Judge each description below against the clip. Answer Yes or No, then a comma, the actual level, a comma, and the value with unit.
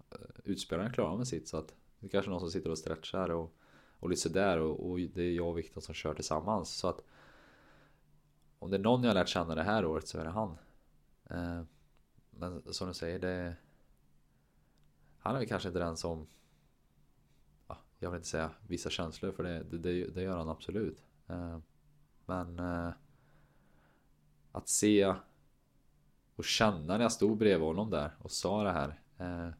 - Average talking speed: Yes, average, 185 wpm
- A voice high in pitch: No, very low, 85 Hz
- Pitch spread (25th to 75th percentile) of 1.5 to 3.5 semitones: Yes, average, 2.9 semitones